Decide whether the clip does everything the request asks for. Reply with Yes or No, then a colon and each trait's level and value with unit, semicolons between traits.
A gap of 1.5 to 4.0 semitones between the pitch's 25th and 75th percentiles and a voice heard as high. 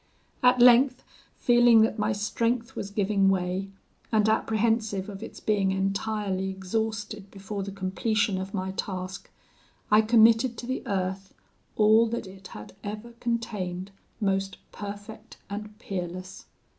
Yes: narrow, 2.6 semitones; high, 205 Hz